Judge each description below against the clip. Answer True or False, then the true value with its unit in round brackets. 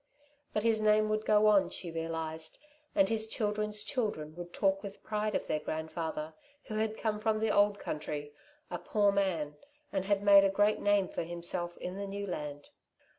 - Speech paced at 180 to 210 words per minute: True (185 wpm)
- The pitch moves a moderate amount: True (4.3 semitones)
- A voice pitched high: True (200 Hz)